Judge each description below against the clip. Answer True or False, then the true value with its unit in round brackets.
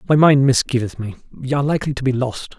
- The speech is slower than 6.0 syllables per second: False (7.0 syllables/s)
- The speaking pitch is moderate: False (130 Hz)